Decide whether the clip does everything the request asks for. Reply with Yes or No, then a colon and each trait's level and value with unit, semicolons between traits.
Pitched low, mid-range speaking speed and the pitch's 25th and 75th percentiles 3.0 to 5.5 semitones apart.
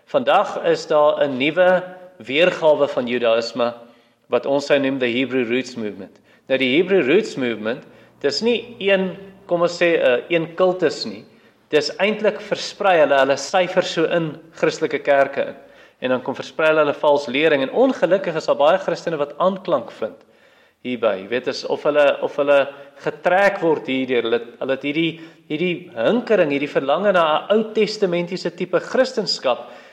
No: medium, 155 Hz; average, 170 wpm; average, 5.2 semitones